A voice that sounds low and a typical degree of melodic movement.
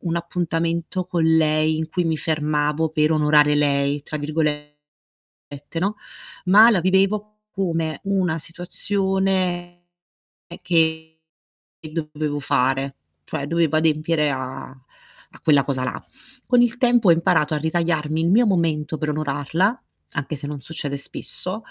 No: medium, 160 Hz; average, 3.0 semitones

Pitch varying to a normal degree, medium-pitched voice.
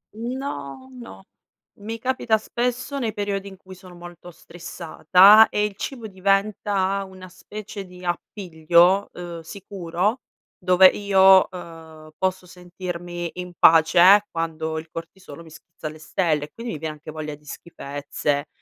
Yes: average, 3.5 semitones; medium, 180 Hz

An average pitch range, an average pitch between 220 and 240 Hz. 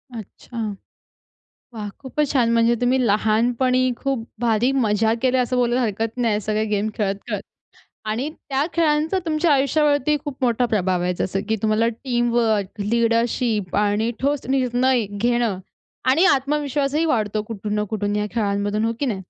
Yes: average, 3.7 semitones; high, 235 Hz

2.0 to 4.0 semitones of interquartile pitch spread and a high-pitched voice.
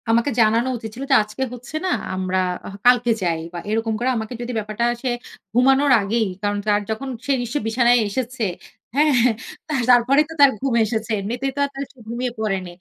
Yes: average, 3.3 semitones; high, 235 Hz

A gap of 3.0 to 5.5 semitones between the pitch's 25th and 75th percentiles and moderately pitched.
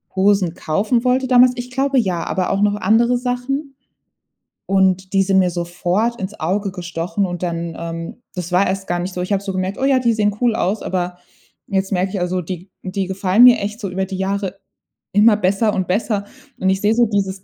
No: average, 3.3 semitones; high, 195 Hz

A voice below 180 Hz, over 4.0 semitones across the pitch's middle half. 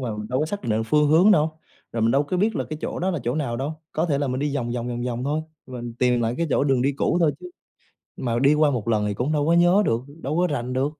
Yes: low, 135 Hz; average, 4.4 semitones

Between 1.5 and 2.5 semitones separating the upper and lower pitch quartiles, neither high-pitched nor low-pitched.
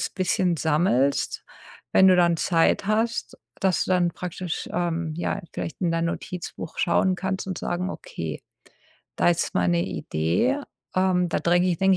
Yes: narrow, 2.1 semitones; medium, 175 Hz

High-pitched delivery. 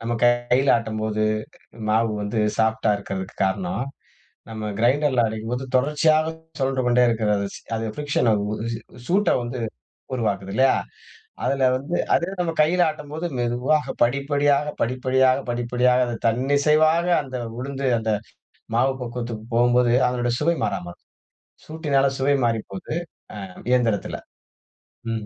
No: low, 125 Hz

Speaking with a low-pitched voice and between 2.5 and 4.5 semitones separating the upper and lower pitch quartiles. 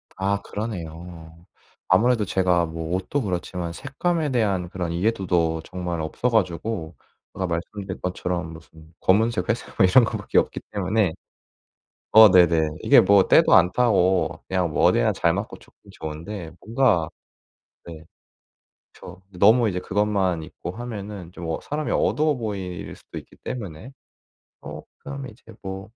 Yes: very low, 95 Hz; average, 4.2 semitones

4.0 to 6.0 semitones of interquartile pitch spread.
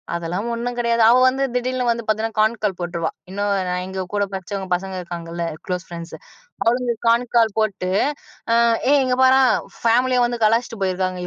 Yes: average, 4.6 semitones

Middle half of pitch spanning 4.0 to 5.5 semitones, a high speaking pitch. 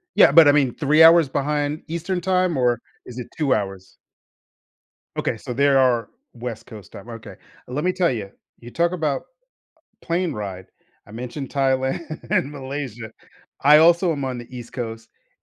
No: average, 4.7 semitones; low, 135 Hz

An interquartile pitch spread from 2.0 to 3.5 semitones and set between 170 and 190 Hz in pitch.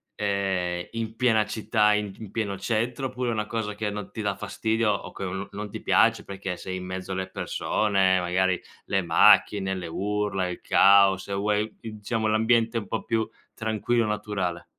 No: narrow, 2.4 semitones; low, 105 Hz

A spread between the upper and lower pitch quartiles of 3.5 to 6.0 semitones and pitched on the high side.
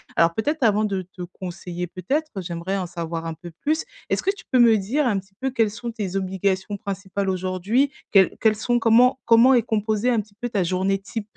Yes: average, 4.1 semitones; high, 200 Hz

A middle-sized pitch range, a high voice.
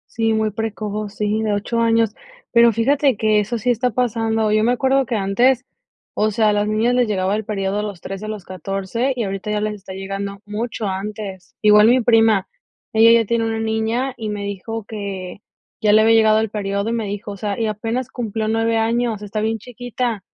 No: narrow, 1.9 semitones; high, 215 Hz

